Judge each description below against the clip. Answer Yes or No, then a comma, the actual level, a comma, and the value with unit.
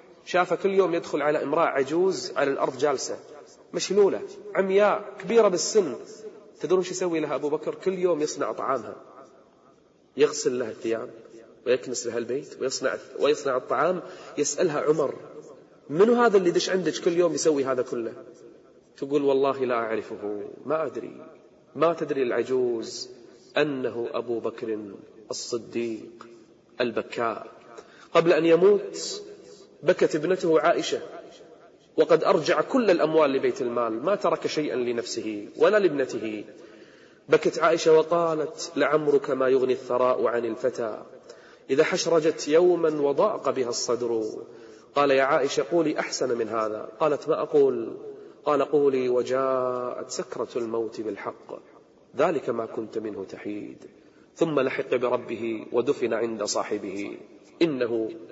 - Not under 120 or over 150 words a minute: Yes, average, 125 wpm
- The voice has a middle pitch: Yes, medium, 180 Hz